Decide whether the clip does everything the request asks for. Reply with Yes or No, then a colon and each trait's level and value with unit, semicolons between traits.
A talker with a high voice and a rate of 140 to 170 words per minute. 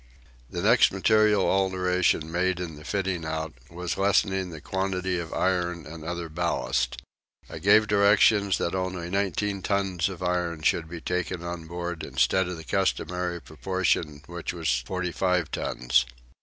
No: very low, 90 Hz; average, 155 wpm